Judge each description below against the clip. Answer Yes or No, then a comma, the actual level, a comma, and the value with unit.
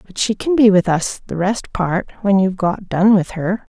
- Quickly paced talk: Yes, fast, 240 wpm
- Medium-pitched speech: No, high, 195 Hz